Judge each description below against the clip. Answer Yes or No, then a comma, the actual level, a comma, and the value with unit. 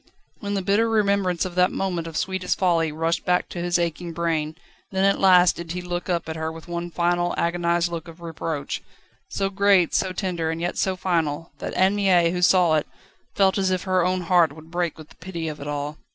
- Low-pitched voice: No, medium, 175 Hz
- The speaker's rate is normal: No, fast, 225 wpm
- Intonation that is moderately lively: No, narrow, 2.1 semitones